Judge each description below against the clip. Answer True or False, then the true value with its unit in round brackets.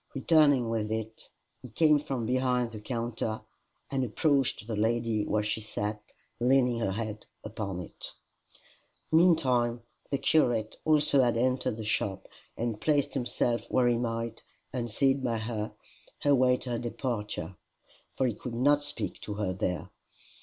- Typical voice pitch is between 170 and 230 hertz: False (120 Hz)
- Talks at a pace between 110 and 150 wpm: True (145 wpm)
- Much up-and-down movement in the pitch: False (3.2 semitones)